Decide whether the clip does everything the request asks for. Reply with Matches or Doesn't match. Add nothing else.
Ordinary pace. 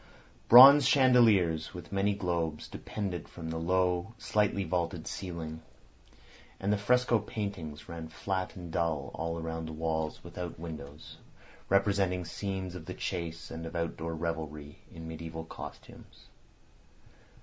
Doesn't match